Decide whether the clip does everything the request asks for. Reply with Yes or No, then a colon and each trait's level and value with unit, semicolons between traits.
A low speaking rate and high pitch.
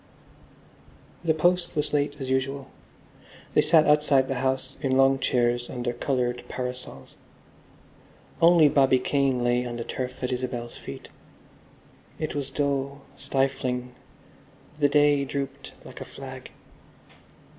No: slow, 125 wpm; low, 135 Hz